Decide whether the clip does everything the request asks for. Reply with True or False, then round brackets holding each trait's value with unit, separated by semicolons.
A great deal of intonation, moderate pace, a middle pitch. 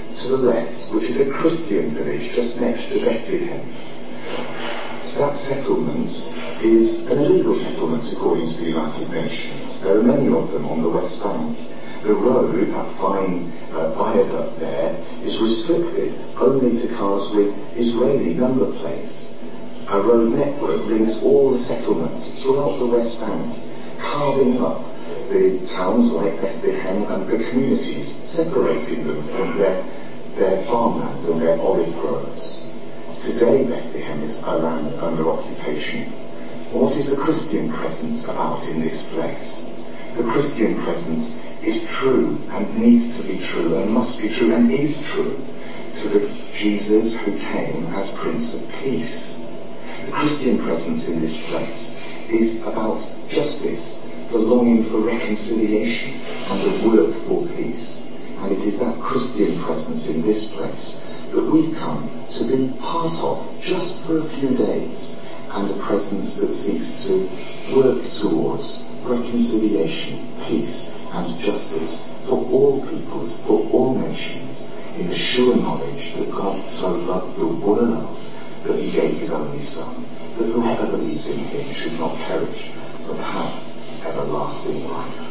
False (6.9 semitones; 145 wpm; 110 Hz)